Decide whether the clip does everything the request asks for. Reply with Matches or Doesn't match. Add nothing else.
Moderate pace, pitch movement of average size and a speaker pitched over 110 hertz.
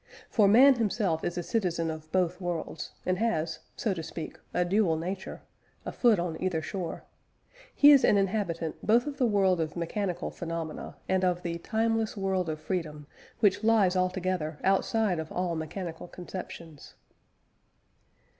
Matches